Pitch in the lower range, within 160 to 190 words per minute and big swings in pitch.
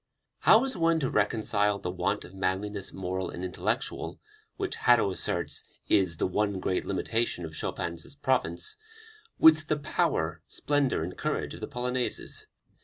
No: low, 100 Hz; average, 150 wpm; wide, 6.2 semitones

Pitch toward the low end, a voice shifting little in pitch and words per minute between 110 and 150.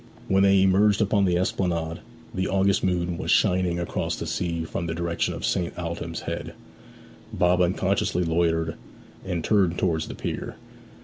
No: very low, 90 Hz; narrow, 2.2 semitones; average, 160 wpm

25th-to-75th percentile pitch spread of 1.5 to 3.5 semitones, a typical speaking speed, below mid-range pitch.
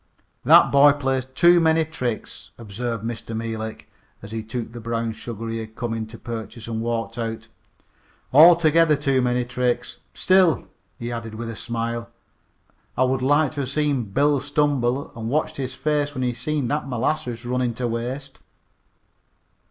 No: average, 3.9 semitones; average, 165 wpm; low, 125 Hz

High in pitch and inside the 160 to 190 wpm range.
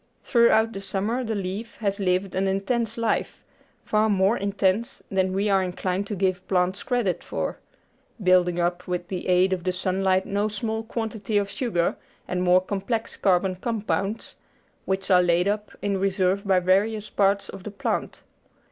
Yes: high, 195 Hz; average, 165 wpm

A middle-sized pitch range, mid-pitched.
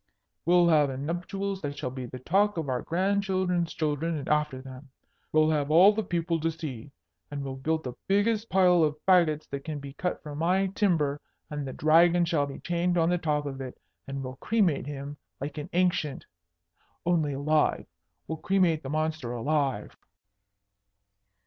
Yes: average, 3.7 semitones; medium, 155 Hz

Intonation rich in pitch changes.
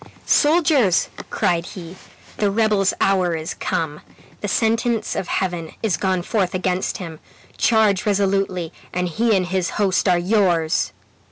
No: average, 3.2 semitones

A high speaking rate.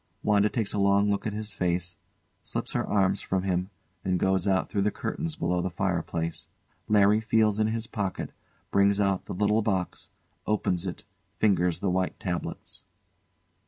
No: average, 165 wpm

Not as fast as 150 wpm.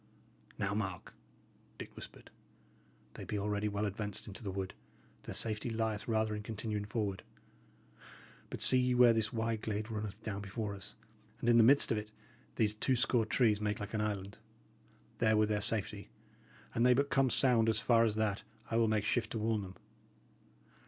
No: average, 185 wpm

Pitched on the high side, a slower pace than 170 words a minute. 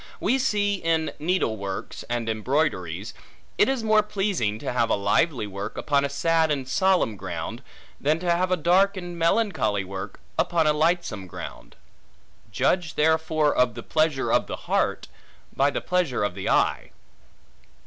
No: medium, 155 Hz; average, 160 wpm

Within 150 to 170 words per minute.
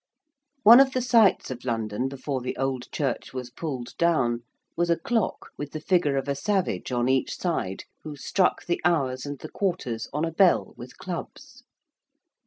No: average, 180 wpm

